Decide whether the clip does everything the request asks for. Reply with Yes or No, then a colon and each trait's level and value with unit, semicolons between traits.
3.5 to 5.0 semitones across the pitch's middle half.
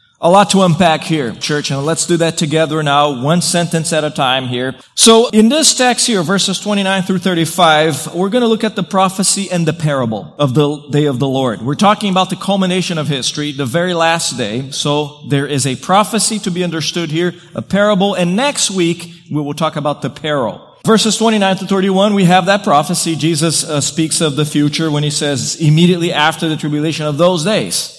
Yes: average, 4.4 semitones